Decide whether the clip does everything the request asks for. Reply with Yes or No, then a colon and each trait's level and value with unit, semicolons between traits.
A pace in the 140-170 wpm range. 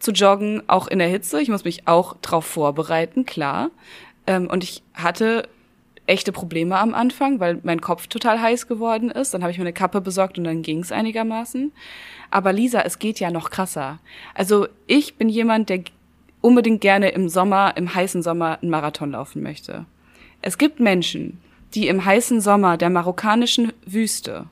No: average, 180 wpm